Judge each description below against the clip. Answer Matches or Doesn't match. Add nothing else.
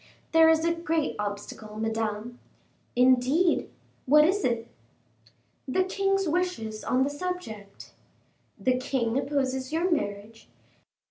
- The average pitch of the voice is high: Matches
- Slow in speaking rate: Matches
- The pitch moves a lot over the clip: Matches